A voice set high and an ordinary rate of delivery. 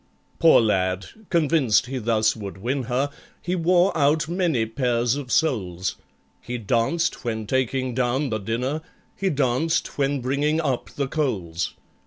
No: low, 130 Hz; average, 145 wpm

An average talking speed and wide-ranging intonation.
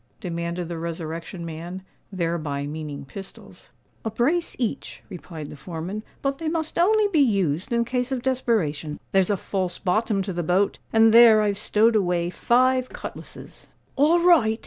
Yes: average, 160 wpm; wide, 6.1 semitones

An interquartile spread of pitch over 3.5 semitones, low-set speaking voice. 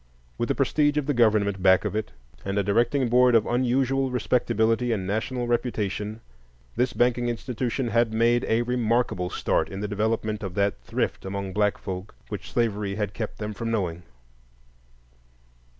No: average, 3.1 semitones; low, 115 Hz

